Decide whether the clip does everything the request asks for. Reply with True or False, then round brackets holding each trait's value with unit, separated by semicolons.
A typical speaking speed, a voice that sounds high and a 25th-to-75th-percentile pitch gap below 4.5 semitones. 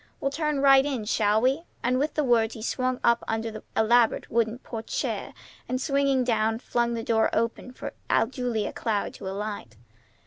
True (180 wpm; 235 Hz; 2.8 semitones)